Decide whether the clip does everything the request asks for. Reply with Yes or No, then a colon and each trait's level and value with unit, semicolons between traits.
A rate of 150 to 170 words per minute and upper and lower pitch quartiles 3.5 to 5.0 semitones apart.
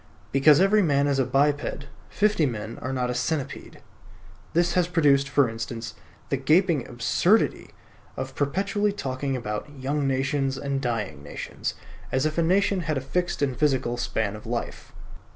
Yes: average, 160 wpm; average, 4.2 semitones